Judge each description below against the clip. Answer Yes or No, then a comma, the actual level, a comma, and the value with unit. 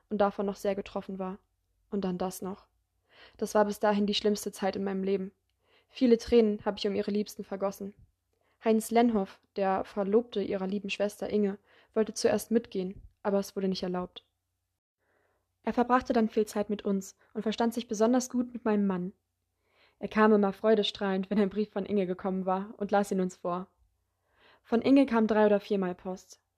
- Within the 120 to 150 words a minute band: No, average, 185 wpm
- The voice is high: Yes, high, 205 Hz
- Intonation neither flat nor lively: No, narrow, 2.2 semitones